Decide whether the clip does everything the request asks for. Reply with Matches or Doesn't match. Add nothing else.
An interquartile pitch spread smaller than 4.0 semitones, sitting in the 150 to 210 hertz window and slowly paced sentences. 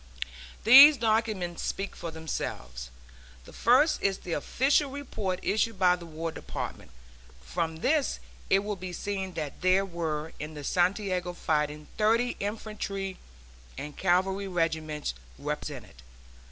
Doesn't match